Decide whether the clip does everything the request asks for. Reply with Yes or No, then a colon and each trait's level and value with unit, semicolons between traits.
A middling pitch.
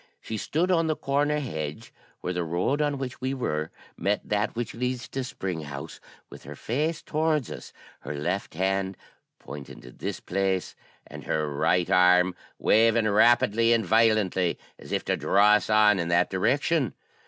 No: low, 105 Hz